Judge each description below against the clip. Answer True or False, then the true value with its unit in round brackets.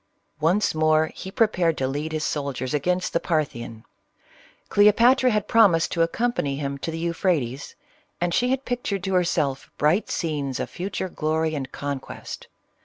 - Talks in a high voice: False (165 Hz)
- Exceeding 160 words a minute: False (155 wpm)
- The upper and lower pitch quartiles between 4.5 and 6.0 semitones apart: True (5.0 semitones)